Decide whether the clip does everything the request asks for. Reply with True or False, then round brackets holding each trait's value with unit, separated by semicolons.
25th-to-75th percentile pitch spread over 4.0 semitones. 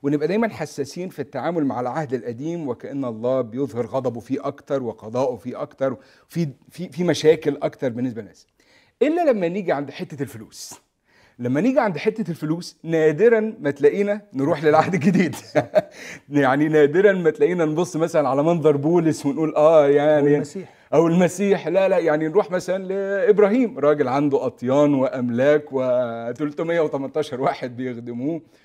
True (4.8 semitones)